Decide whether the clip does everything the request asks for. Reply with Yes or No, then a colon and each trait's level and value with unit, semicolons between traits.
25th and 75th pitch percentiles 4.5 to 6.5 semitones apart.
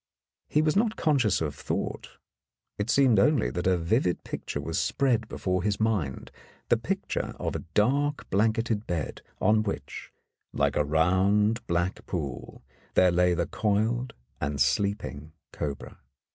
Yes: average, 4.8 semitones